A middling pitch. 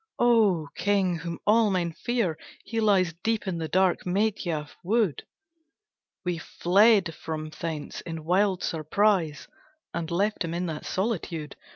Yes: medium, 180 Hz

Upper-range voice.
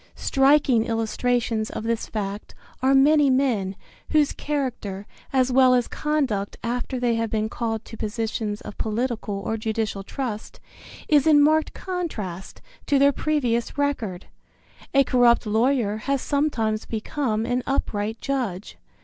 Yes: high, 235 Hz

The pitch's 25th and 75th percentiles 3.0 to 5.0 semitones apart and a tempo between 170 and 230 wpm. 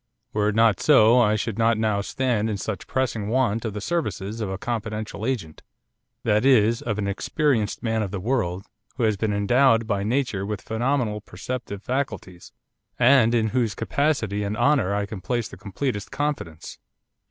Yes: average, 3.5 semitones; average, 175 wpm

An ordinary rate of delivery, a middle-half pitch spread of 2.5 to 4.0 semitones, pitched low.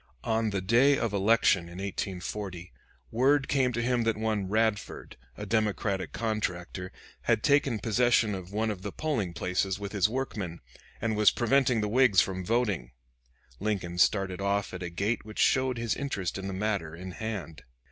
Yes: average, 170 wpm; average, 3.6 semitones; low, 105 Hz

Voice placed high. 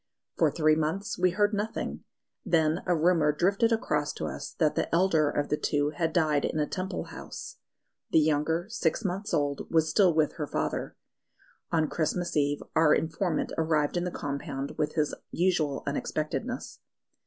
No: medium, 160 Hz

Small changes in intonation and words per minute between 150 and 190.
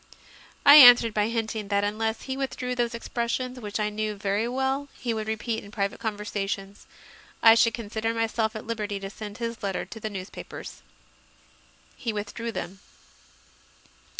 Yes: narrow, 2.2 semitones; average, 155 wpm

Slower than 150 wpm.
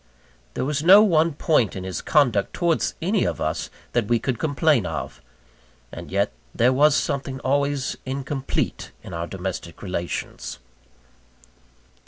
Yes: average, 140 wpm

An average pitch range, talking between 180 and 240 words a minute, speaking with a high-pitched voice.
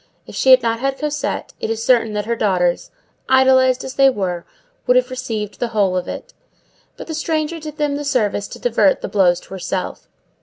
Yes: average, 4.9 semitones; fast, 205 wpm; high, 240 Hz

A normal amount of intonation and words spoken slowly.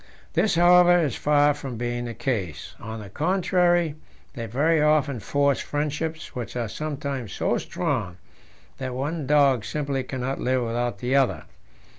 No: average, 4.0 semitones; average, 150 wpm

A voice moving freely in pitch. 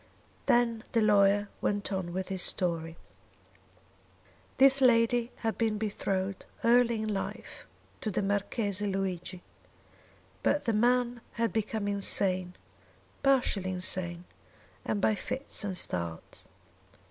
No: average, 3.6 semitones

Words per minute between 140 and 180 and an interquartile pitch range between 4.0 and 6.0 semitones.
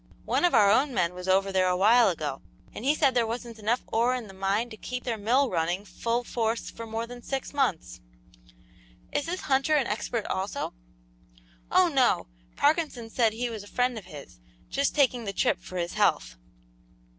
No: average, 195 wpm; average, 4.5 semitones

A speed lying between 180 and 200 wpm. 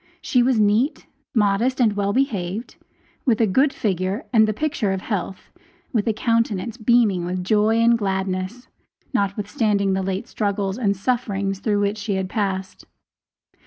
No: average, 155 wpm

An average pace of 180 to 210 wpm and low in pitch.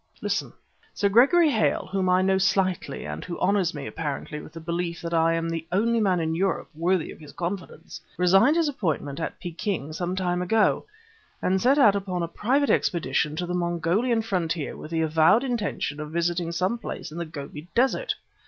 No: average, 190 wpm; medium, 180 Hz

